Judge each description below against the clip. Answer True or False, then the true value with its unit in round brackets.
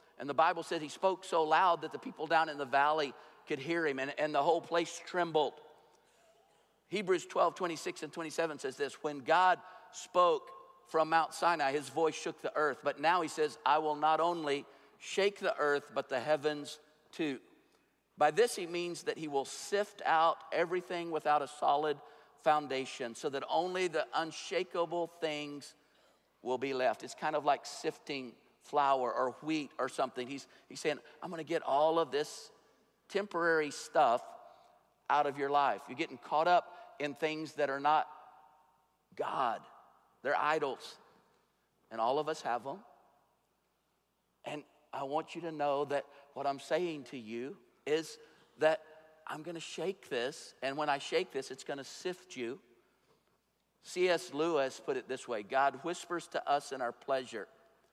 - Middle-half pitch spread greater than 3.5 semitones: False (3.0 semitones)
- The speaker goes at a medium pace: True (170 wpm)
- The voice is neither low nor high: True (155 Hz)